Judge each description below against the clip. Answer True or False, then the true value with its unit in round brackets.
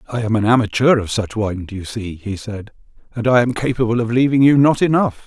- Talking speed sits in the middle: False (240 wpm)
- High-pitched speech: False (115 Hz)